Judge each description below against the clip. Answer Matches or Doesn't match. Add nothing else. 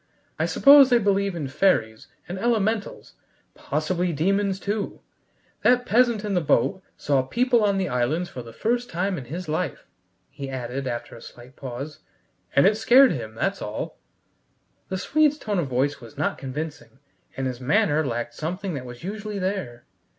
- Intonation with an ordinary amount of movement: Doesn't match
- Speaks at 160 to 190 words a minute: Matches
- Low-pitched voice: Doesn't match